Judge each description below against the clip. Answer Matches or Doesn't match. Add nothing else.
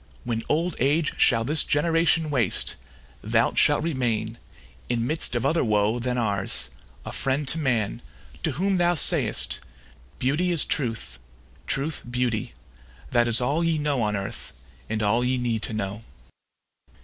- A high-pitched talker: Doesn't match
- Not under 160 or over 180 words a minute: Doesn't match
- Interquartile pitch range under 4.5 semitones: Doesn't match